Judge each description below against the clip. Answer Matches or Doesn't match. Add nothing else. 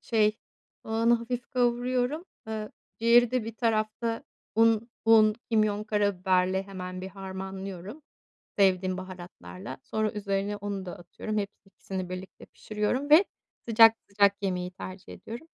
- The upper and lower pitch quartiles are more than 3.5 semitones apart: Doesn't match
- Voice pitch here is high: Matches